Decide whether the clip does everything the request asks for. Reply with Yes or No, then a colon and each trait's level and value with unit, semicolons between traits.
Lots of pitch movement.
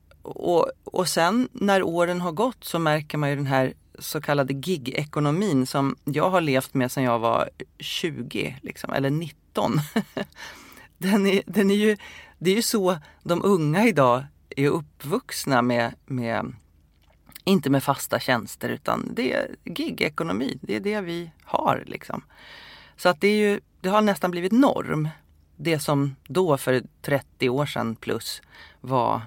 Yes: wide, 6.3 semitones